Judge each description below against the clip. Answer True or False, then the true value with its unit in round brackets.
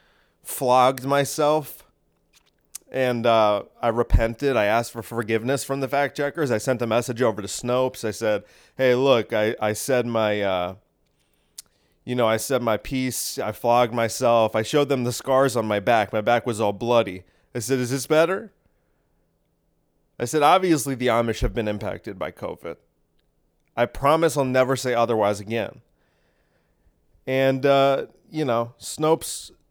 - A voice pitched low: True (120 Hz)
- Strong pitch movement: False (3.6 semitones)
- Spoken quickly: False (160 wpm)